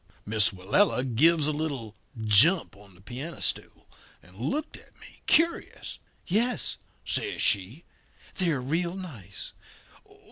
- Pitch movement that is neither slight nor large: No, wide, 8.8 semitones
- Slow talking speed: Yes, slow, 120 wpm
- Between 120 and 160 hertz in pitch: Yes, medium, 140 Hz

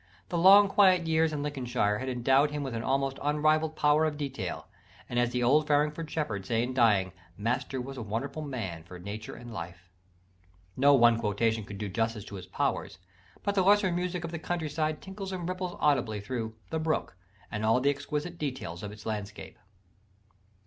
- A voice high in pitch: No, low, 135 Hz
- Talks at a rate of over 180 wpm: Yes, average, 190 wpm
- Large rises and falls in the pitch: Yes, wide, 5.9 semitones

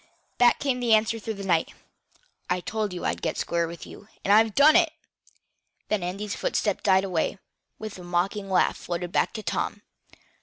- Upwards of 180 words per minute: Yes, average, 190 wpm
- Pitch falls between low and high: No, high, 200 Hz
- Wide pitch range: No, average, 3.7 semitones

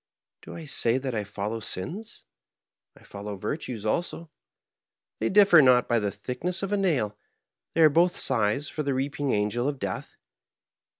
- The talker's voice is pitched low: Yes, low, 130 Hz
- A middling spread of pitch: No, wide, 7.2 semitones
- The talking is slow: No, average, 165 wpm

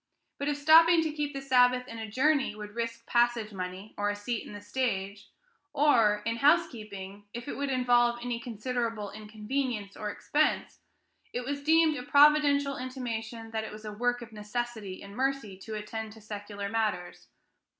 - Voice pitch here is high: Yes, high, 235 Hz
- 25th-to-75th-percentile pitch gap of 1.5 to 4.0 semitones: No, average, 4.4 semitones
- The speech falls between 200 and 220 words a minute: No, average, 175 wpm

